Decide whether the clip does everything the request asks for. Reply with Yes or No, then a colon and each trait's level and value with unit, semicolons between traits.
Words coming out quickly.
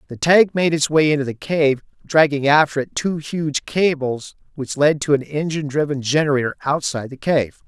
No: average, 190 wpm